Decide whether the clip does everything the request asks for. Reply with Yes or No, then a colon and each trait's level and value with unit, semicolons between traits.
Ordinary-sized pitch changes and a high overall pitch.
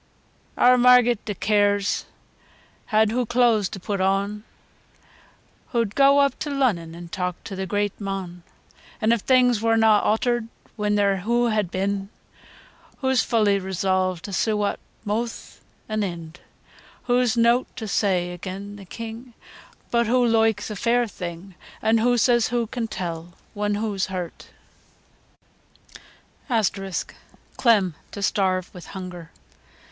Yes: average, 3.6 semitones; high, 210 Hz